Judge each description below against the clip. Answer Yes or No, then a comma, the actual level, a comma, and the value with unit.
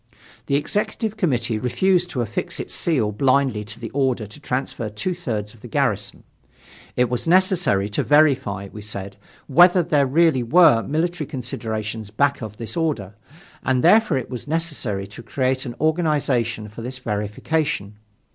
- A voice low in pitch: Yes, low, 130 Hz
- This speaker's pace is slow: No, average, 155 wpm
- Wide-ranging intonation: Yes, wide, 6.5 semitones